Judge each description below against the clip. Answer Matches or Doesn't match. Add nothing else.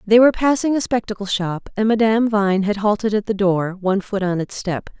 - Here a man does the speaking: Doesn't match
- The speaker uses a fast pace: Matches